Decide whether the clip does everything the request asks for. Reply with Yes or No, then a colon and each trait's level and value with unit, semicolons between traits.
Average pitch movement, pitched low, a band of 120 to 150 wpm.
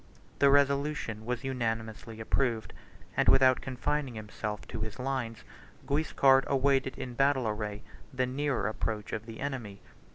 Yes: average, 3.7 semitones; low, 125 Hz; slow, 135 wpm